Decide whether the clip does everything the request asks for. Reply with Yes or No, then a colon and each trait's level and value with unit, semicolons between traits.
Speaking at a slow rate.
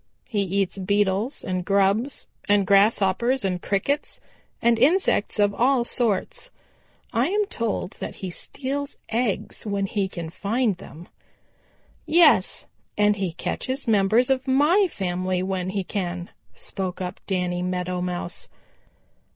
Yes: slow, 130 wpm